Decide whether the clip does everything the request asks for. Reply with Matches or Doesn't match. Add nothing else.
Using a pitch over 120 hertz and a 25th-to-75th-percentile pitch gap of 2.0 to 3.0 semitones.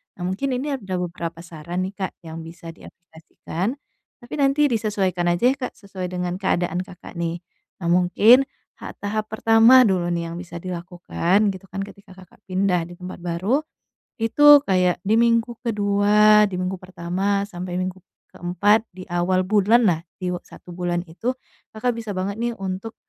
Doesn't match